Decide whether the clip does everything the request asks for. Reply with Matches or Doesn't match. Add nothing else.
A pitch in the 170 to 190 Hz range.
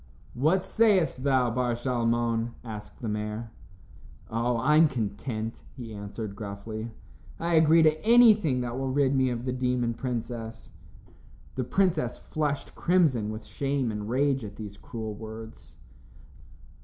Doesn't match